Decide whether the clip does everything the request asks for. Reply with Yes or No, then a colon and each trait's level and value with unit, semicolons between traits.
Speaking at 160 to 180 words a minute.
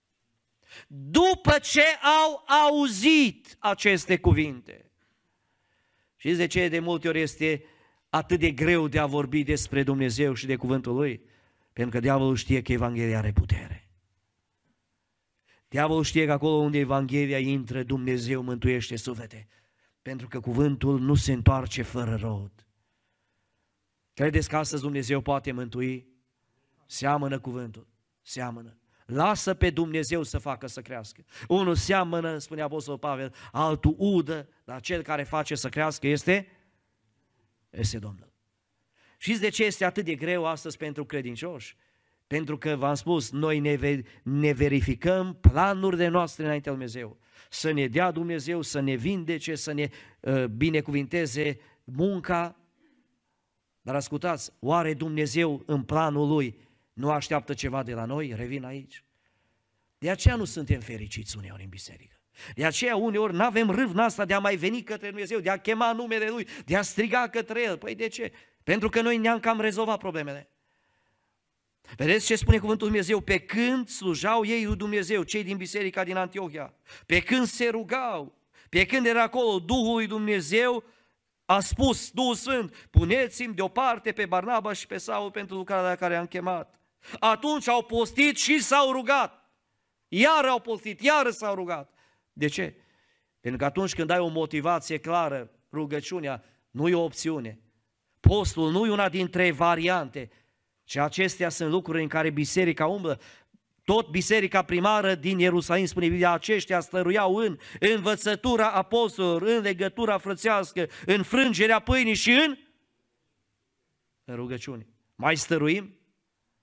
No: average, 145 wpm